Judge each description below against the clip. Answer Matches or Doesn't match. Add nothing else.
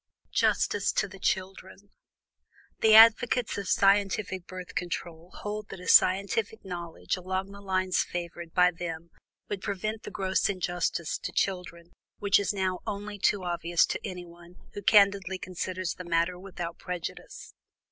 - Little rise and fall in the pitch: Matches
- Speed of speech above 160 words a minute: Doesn't match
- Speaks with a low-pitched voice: Doesn't match